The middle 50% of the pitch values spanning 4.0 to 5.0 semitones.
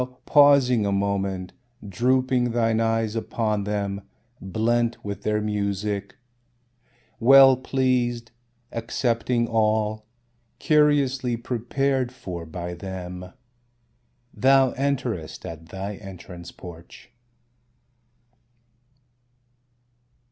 Yes: average, 4.3 semitones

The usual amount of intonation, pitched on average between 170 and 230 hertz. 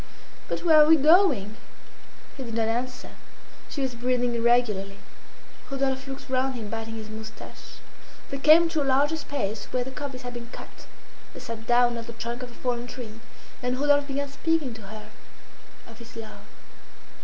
No: average, 3.2 semitones; high, 245 Hz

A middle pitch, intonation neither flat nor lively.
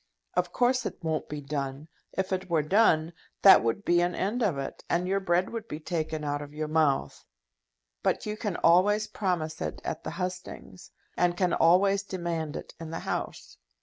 Yes: medium, 175 Hz; average, 3.6 semitones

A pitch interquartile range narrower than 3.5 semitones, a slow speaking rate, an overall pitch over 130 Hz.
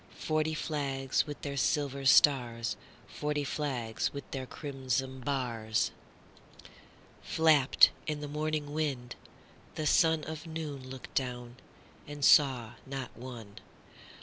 Yes: average, 2.7 semitones; slow, 100 wpm; medium, 140 Hz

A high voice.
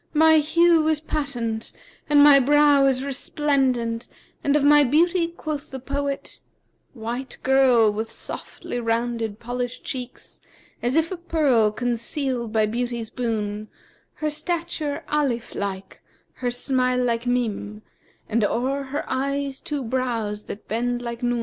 Yes: very high, 255 Hz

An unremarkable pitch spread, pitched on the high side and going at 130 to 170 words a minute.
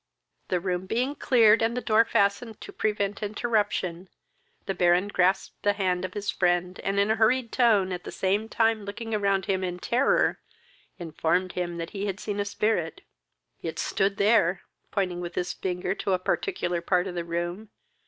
No: average, 3.2 semitones; high, 195 Hz; average, 185 wpm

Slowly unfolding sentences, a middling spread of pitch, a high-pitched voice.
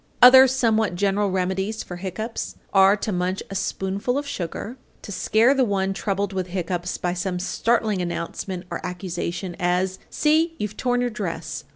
No: average, 165 wpm; average, 3.5 semitones; high, 195 Hz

